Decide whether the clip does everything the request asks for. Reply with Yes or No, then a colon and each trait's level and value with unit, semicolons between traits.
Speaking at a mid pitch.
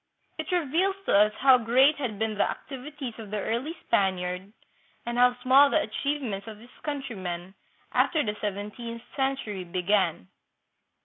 No: high, 230 Hz